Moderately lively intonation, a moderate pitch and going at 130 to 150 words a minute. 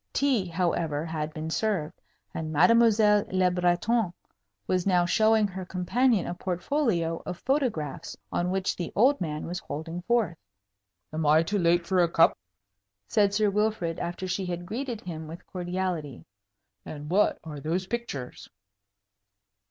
Yes: average, 4.0 semitones; medium, 180 Hz; average, 145 wpm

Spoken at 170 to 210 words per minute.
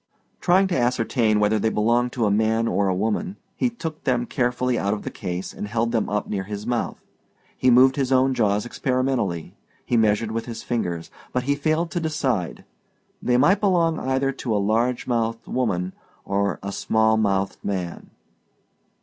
Yes: average, 180 wpm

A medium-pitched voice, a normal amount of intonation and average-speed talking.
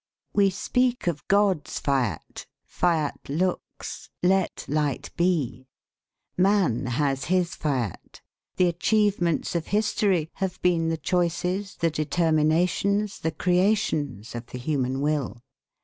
No: medium, 170 Hz; average, 4.5 semitones; slow, 115 wpm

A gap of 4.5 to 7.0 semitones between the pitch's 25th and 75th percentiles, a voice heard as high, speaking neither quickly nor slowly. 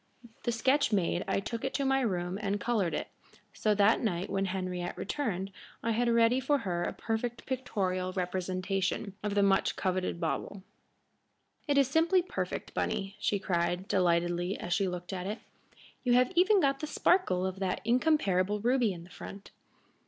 Yes: average, 4.8 semitones; high, 200 Hz; average, 175 wpm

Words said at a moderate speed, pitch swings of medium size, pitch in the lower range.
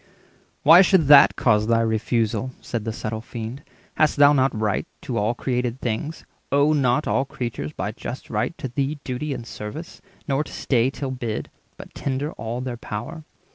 Yes: average, 175 wpm; average, 3.9 semitones; low, 125 Hz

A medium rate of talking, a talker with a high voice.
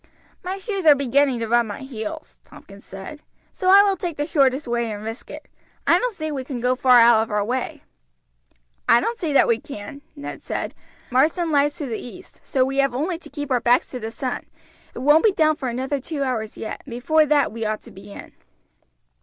No: fast, 225 wpm; very high, 270 Hz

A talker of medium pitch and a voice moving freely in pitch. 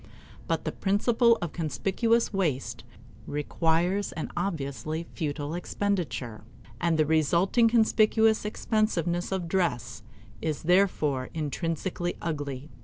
No: medium, 170 Hz; average, 4.8 semitones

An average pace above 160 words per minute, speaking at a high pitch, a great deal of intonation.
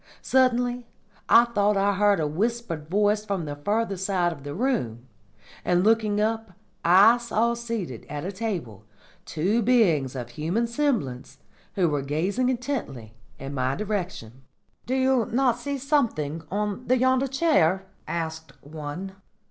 No: average, 140 wpm; high, 200 Hz; wide, 7.1 semitones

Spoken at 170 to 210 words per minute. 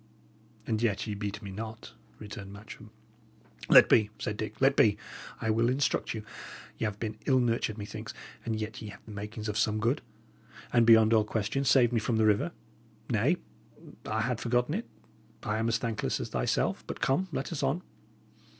Yes: average, 185 wpm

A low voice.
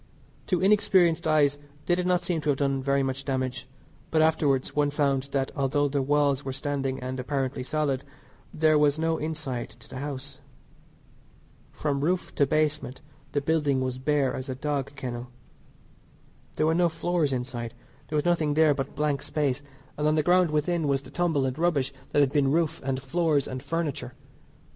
No: medium, 145 Hz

